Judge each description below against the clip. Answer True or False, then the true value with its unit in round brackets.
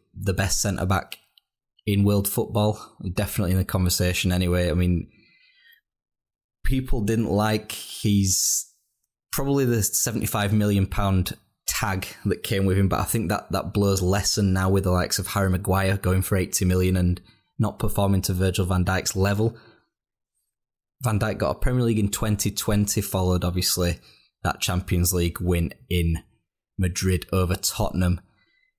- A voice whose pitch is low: True (95 Hz)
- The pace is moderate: True (155 wpm)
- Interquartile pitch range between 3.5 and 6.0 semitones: False (2.7 semitones)